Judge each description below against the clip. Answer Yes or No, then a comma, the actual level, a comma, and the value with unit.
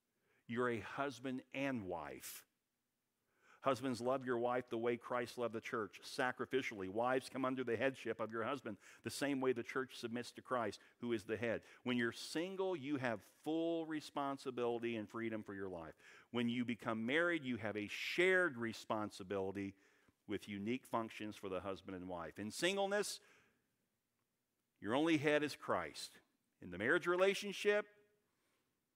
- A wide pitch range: No, average, 4.0 semitones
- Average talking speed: Yes, average, 155 wpm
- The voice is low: Yes, low, 125 Hz